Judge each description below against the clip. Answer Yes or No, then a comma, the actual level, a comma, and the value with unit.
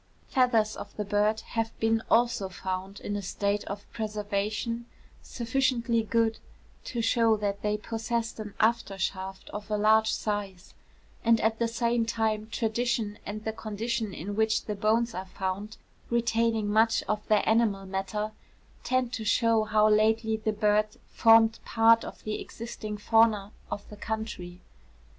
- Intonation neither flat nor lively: No, narrow, 1.7 semitones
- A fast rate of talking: No, average, 150 wpm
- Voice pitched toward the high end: Yes, high, 215 Hz